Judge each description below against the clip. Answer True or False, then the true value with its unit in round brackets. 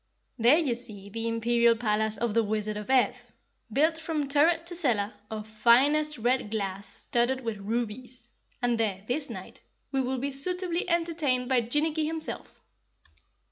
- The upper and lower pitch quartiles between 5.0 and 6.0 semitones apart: True (5.4 semitones)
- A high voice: True (245 Hz)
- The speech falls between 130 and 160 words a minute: True (155 wpm)